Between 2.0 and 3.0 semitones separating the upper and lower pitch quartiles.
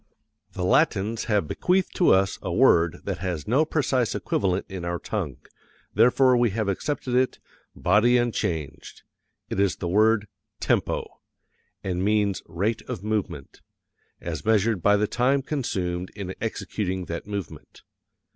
No: average, 4.4 semitones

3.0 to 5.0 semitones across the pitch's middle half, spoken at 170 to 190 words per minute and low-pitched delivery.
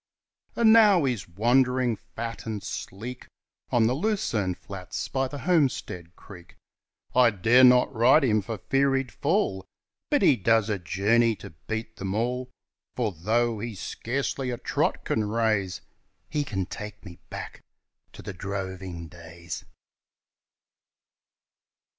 No: average, 4.7 semitones; slow, 135 wpm; low, 115 Hz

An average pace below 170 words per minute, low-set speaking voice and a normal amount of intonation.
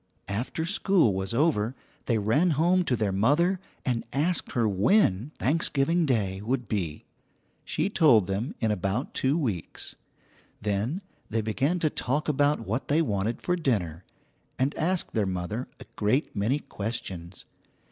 No: average, 145 wpm; low, 120 Hz; wide, 7.0 semitones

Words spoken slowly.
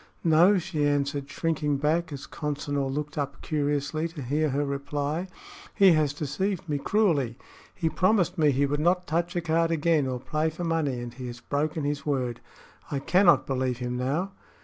No: average, 180 wpm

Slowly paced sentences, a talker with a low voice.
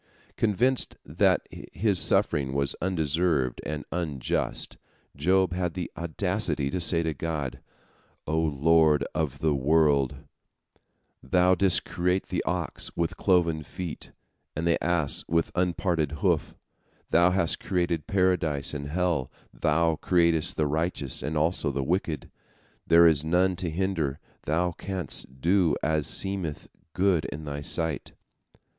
Yes: slow, 130 wpm; very low, 80 Hz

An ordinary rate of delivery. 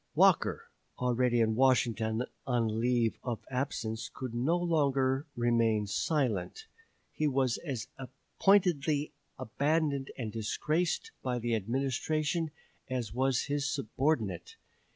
No: slow, 110 wpm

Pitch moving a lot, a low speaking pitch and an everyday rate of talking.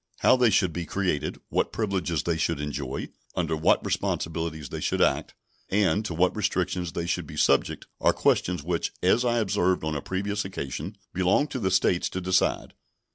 No: average, 3.3 semitones; very low, 90 Hz; average, 185 wpm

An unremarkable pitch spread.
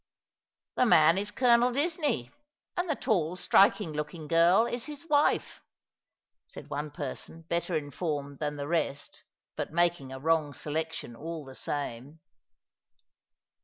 No: wide, 5.9 semitones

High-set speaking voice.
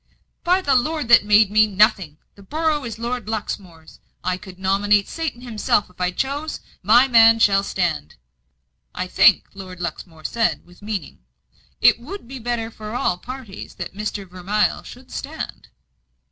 Yes: high, 210 Hz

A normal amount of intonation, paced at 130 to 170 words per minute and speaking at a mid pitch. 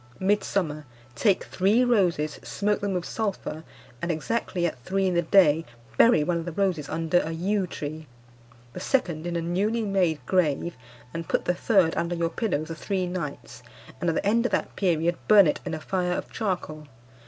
No: average, 3.5 semitones; average, 190 wpm; medium, 175 Hz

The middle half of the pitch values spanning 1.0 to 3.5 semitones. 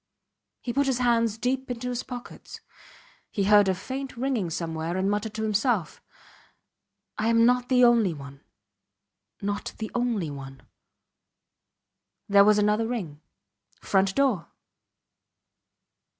No: average, 4.4 semitones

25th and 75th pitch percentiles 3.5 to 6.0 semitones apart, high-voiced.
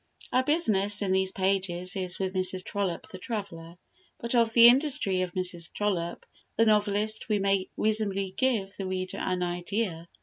No: average, 2.7 semitones; high, 195 Hz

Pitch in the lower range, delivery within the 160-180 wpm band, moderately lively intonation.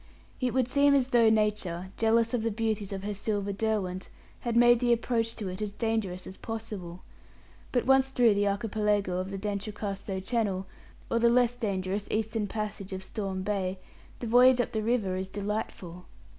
No: high, 210 Hz; average, 175 wpm; average, 3.0 semitones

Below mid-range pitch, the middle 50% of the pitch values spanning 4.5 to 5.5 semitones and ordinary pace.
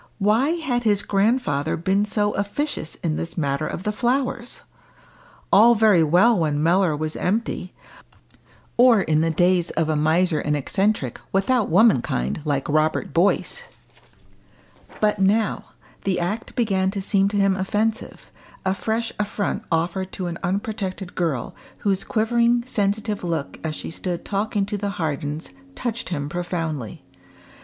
No: high, 195 Hz; average, 4.8 semitones; average, 145 wpm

